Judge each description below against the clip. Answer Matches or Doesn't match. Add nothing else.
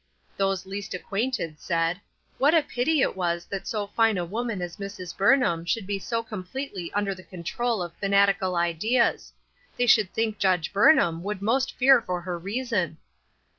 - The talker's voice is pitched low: Doesn't match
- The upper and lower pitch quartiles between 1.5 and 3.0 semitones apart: Doesn't match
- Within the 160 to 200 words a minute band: Matches